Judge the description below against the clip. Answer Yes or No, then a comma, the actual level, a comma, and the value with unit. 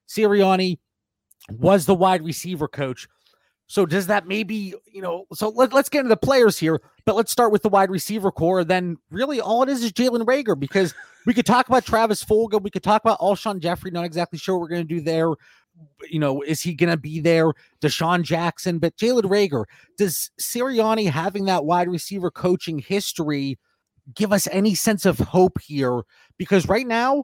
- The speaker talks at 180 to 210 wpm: Yes, average, 195 wpm